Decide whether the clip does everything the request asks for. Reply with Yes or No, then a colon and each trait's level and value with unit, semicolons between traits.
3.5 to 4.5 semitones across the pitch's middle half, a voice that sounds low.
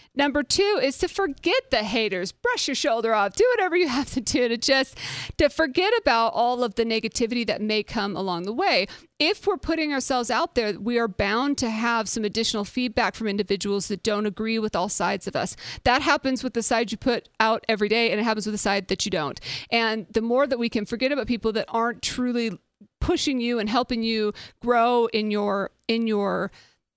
No: average, 3.8 semitones; high, 230 Hz